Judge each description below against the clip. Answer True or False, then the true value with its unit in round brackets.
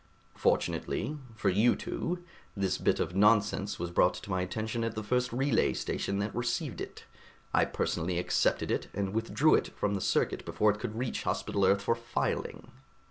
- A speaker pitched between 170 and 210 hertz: False (105 Hz)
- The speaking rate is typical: True (180 wpm)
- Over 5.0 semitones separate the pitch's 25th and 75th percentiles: False (3.3 semitones)